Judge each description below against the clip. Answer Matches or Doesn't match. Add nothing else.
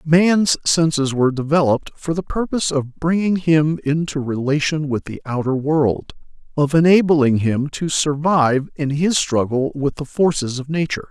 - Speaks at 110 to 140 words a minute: Doesn't match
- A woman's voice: Doesn't match